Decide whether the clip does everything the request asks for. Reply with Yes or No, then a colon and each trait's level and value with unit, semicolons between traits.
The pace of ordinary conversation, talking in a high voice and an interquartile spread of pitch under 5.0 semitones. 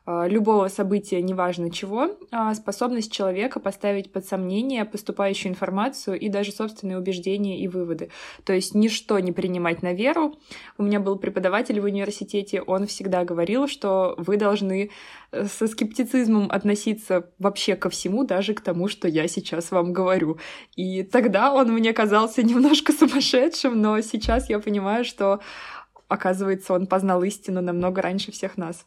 Yes: average, 145 wpm; high, 200 Hz; average, 2.9 semitones